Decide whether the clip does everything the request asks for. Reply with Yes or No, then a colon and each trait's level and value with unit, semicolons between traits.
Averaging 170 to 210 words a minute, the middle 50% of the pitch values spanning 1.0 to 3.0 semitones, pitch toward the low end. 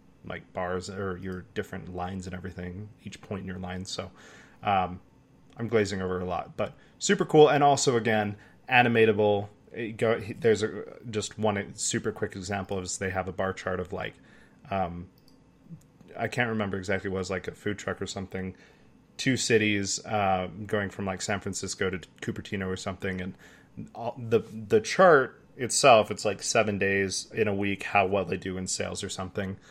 Yes: average, 180 wpm; narrow, 2.5 semitones; low, 100 Hz